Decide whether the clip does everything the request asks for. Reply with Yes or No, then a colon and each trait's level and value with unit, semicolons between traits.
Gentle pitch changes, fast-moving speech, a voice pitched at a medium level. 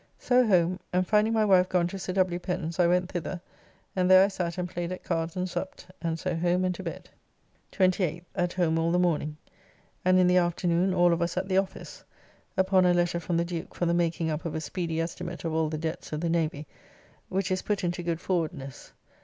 Yes: narrow, 1.7 semitones; fast, 230 wpm; medium, 175 Hz